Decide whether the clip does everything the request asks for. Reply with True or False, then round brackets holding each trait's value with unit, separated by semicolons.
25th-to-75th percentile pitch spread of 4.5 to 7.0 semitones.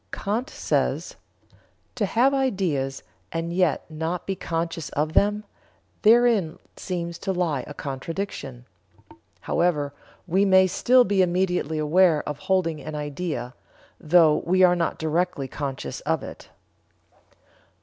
False (3.8 semitones)